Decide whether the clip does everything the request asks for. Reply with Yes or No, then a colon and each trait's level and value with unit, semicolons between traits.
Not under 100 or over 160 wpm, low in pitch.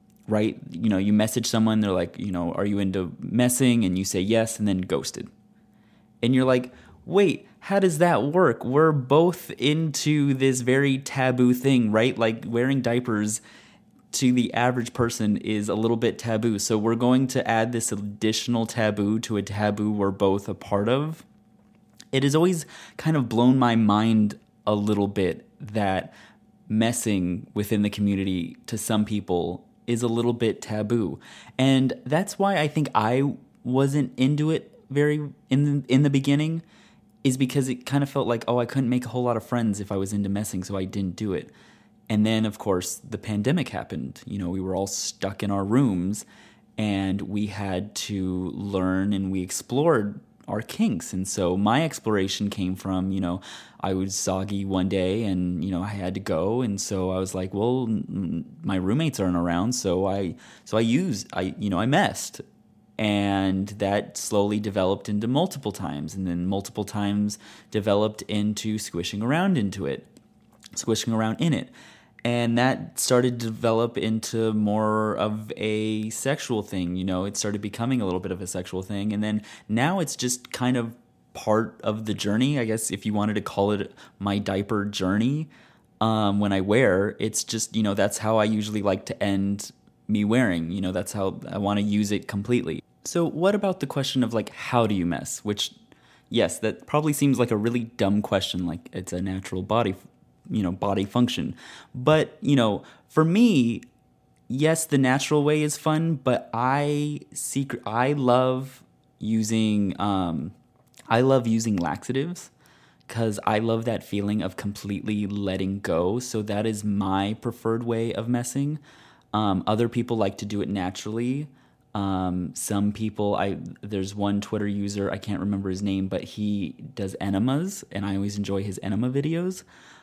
No: average, 180 wpm; low, 110 Hz